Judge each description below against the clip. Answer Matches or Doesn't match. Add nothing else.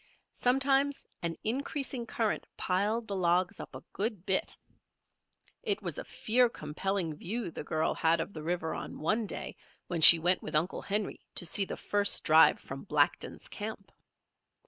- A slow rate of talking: Doesn't match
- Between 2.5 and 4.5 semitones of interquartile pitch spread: Doesn't match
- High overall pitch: Matches